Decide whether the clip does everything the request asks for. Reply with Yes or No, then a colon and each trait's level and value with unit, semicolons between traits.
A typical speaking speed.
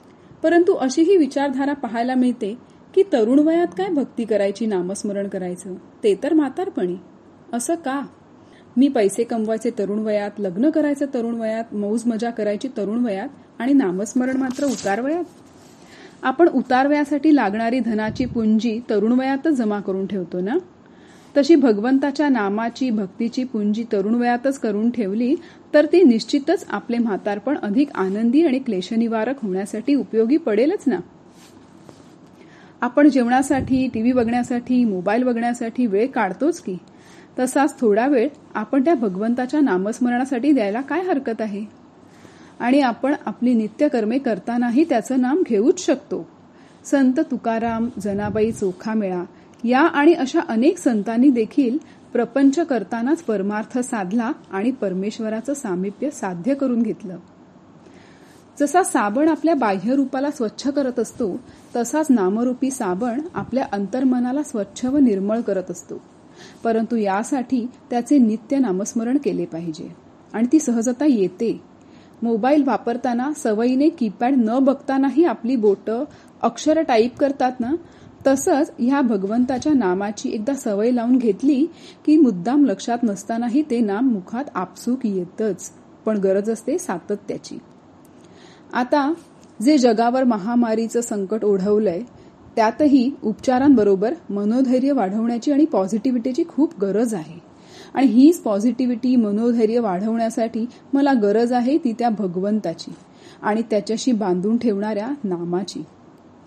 Yes: average, 120 wpm